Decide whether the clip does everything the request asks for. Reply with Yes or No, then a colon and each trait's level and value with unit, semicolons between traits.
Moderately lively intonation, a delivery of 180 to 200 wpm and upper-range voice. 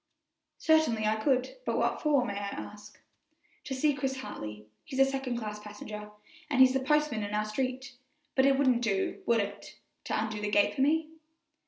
Yes: average, 4.4 semitones; average, 190 wpm; very high, 250 Hz